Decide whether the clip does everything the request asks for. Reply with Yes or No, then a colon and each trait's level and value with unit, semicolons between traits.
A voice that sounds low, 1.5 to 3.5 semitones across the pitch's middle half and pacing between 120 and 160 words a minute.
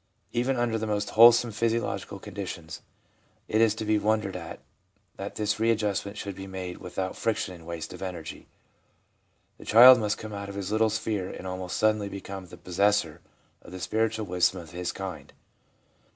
No: low, 100 Hz; average, 3.1 semitones; average, 175 wpm